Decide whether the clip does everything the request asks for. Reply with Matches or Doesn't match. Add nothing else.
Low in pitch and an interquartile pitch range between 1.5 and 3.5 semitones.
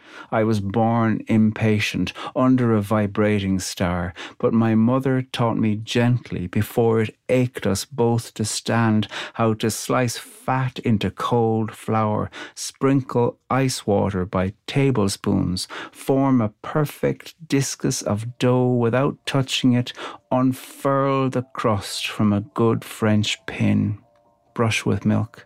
Matches